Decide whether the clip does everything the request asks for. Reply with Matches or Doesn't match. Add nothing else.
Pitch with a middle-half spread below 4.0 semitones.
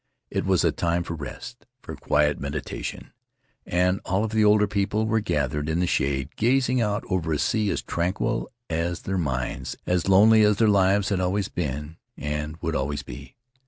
Doesn't match